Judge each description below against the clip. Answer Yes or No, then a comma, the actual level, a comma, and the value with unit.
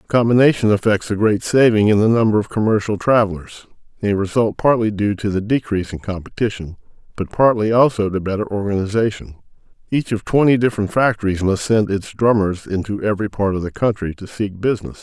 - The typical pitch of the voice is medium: No, low, 105 Hz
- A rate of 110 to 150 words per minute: No, average, 175 wpm